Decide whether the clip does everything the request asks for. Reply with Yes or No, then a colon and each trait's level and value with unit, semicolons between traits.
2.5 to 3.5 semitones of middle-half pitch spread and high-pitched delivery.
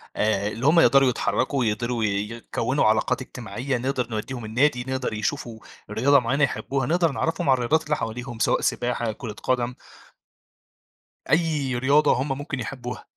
No: average, 3.2 semitones; low, 125 Hz